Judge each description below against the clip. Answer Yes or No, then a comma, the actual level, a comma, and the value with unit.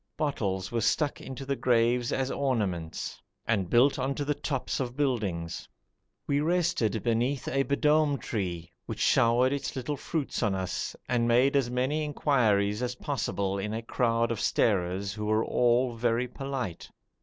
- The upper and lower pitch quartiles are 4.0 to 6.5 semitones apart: Yes, average, 4.5 semitones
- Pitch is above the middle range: No, low, 120 Hz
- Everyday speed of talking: Yes, average, 160 wpm